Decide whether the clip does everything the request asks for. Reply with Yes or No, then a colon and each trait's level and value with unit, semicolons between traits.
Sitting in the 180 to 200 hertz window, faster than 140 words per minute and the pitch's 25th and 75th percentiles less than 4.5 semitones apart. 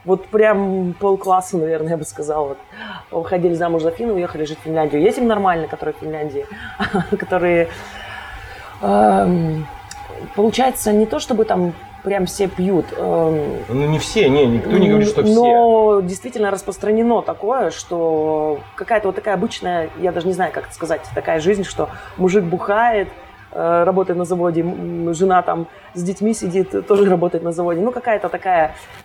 Yes: medium, 185 Hz; average, 155 wpm; average, 3.6 semitones